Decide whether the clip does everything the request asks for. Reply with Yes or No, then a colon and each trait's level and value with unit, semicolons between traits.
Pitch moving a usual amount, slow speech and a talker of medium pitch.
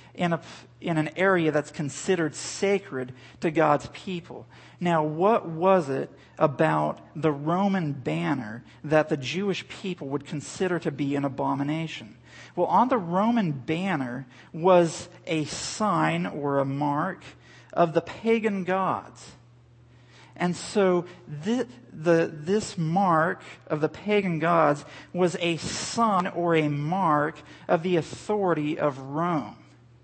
Yes: average, 4.0 semitones; slow, 130 wpm; medium, 160 Hz